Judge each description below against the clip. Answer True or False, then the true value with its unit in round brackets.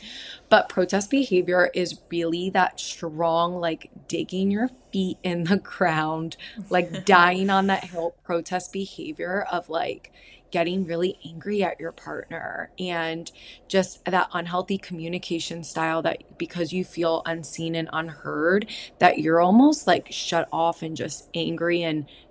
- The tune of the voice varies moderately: False (2.1 semitones)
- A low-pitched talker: False (175 Hz)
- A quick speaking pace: False (140 wpm)